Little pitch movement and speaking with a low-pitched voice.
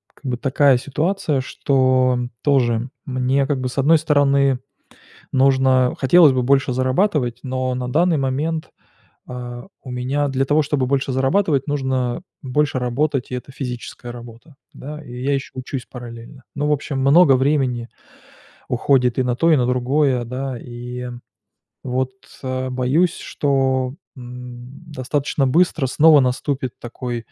Yes: narrow, 2.3 semitones; low, 130 Hz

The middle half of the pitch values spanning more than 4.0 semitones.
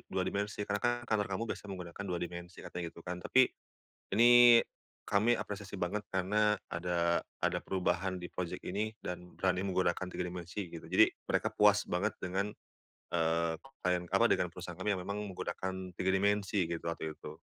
No: average, 2.7 semitones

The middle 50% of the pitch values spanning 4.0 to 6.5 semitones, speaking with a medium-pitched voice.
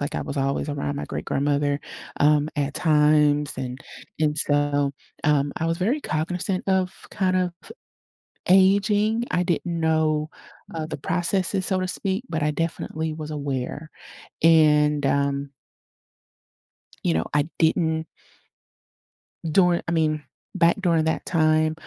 No: average, 3.4 semitones; medium, 155 Hz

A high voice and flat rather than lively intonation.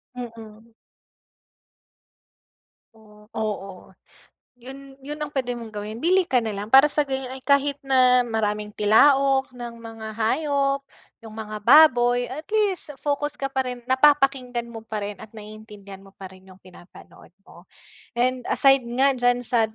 No: high, 245 Hz; average, 4.0 semitones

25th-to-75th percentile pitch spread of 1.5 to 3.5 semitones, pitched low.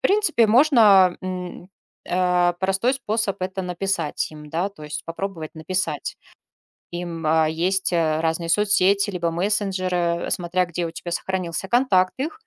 No: narrow, 2.6 semitones; medium, 185 Hz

